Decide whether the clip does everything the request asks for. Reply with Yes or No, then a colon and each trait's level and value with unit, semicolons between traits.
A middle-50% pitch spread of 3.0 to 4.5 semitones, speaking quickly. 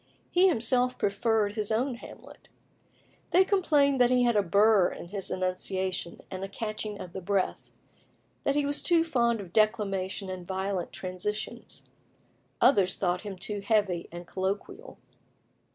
No: average, 4.2 semitones; average, 150 wpm